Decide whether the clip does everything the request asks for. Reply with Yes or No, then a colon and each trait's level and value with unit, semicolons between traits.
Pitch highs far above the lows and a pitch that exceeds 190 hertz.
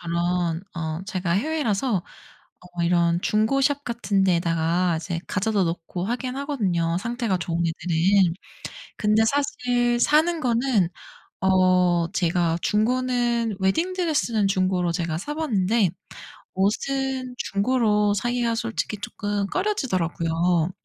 Yes: wide, 5.7 semitones; high, 200 Hz